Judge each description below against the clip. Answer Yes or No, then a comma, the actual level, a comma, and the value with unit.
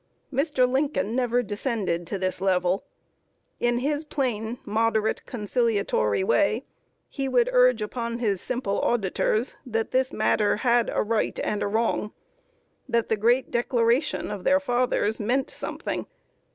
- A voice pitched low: No, high, 230 Hz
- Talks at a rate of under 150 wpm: Yes, average, 140 wpm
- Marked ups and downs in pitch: No, average, 3.2 semitones